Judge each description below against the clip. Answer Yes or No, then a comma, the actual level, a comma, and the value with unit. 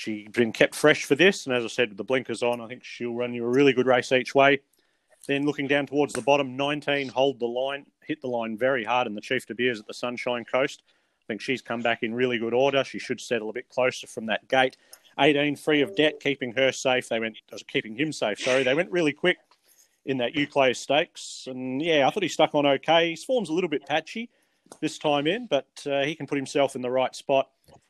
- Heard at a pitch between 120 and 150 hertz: Yes, low, 135 Hz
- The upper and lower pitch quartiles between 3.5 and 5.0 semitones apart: No, average, 2.8 semitones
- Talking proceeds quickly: Yes, fast, 250 wpm